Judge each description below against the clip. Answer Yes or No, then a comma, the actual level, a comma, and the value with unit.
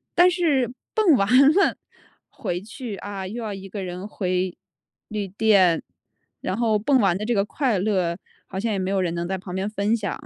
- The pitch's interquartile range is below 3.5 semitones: No, average, 3.8 semitones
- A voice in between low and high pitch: No, high, 200 Hz